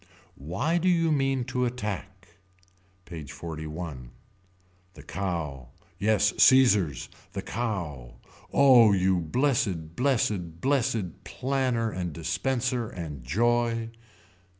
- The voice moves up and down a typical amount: No, wide, 7.1 semitones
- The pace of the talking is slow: Yes, slow, 100 wpm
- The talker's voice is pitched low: Yes, low, 100 Hz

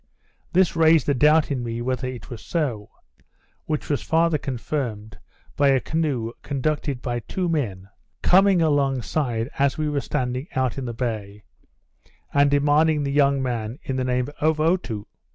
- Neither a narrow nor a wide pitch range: Yes, average, 3.9 semitones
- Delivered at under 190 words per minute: Yes, average, 165 wpm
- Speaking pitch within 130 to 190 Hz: Yes, medium, 140 Hz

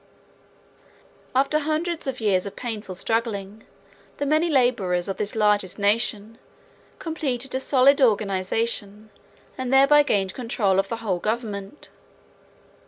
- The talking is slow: Yes, slow, 120 wpm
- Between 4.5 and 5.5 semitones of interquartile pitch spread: Yes, average, 5.0 semitones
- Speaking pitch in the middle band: No, high, 225 Hz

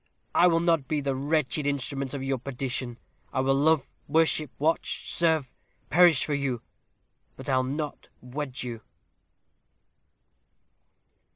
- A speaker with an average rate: No, slow, 125 wpm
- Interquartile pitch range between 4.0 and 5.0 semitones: No, average, 3.0 semitones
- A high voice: No, medium, 140 Hz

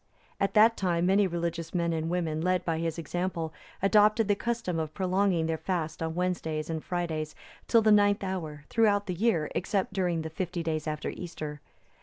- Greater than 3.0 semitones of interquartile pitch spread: Yes, average, 3.4 semitones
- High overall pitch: No, medium, 175 Hz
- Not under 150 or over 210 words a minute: Yes, average, 185 wpm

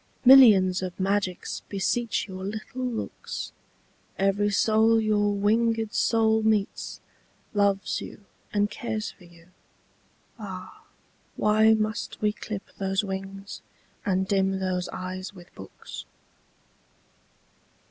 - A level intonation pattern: Yes, narrow, 2.3 semitones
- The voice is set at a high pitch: Yes, high, 205 Hz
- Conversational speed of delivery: No, slow, 105 wpm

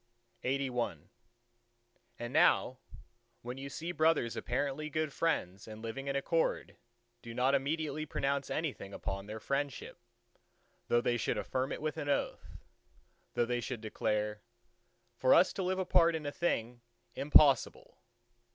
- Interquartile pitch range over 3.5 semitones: Yes, average, 4.5 semitones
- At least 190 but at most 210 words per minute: No, average, 140 wpm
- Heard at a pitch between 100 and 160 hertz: Yes, low, 135 Hz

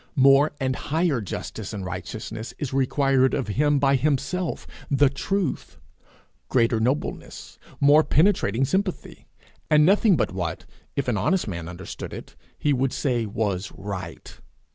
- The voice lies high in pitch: No, low, 135 Hz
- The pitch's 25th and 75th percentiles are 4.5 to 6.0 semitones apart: Yes, wide, 5.5 semitones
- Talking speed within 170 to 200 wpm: No, average, 140 wpm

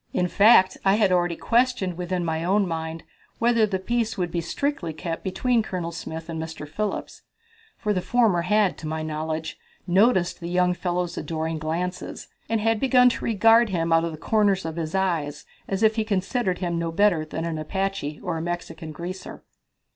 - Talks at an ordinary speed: Yes, average, 190 wpm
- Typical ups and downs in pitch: Yes, average, 4.2 semitones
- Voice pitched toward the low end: No, medium, 180 Hz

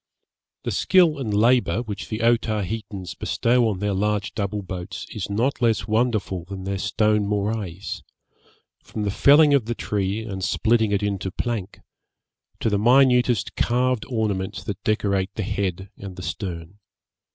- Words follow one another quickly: No, average, 150 wpm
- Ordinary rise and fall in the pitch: Yes, average, 3.0 semitones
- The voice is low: Yes, low, 105 Hz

